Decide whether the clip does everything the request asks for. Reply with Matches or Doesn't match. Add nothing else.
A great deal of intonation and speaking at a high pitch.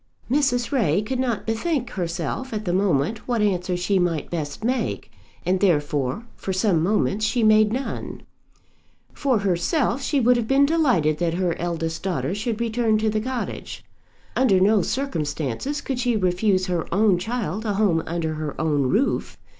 Matches